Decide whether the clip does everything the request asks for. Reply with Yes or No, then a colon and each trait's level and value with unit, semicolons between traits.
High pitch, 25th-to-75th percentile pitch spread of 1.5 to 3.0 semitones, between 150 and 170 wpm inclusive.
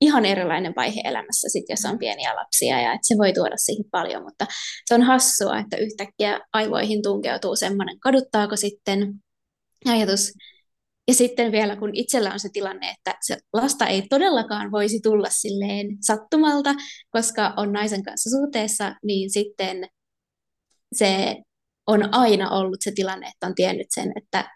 Yes: high, 210 Hz; narrow, 2.5 semitones; fast, 155 wpm